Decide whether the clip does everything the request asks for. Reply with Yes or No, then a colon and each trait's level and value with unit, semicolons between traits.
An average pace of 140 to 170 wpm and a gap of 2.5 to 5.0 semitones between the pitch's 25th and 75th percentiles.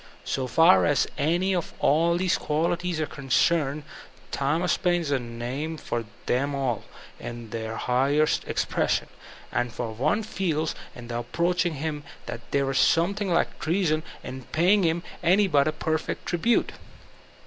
Yes: average, 150 wpm; average, 4.6 semitones